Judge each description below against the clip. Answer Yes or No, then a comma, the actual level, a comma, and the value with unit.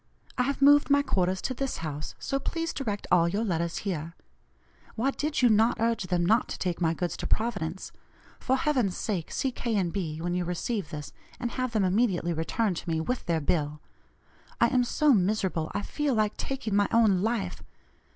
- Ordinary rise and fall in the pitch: No, wide, 6.1 semitones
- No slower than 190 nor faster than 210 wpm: Yes, average, 200 wpm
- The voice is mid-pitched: No, high, 205 Hz